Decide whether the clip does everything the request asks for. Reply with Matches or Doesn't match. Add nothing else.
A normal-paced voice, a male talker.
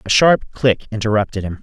Matches